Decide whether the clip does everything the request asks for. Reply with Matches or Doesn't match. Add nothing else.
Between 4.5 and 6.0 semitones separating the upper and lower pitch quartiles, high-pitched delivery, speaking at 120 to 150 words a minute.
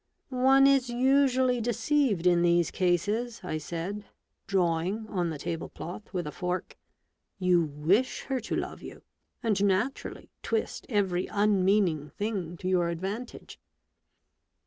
Matches